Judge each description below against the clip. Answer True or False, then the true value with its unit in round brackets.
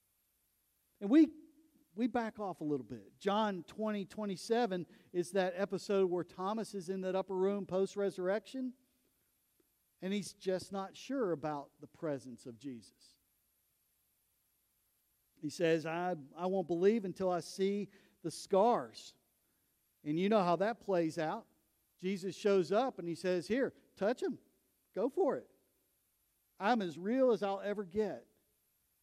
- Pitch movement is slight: False (3.8 semitones)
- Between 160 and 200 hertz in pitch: True (190 Hz)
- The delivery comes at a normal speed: True (145 wpm)